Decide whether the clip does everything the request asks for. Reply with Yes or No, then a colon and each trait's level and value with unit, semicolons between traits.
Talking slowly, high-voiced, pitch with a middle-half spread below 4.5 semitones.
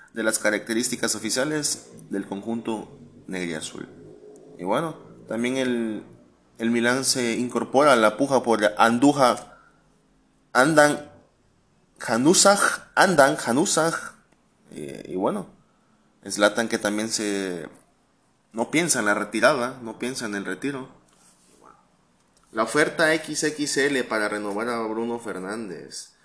No: slow, 115 wpm; low, 115 Hz; average, 3.6 semitones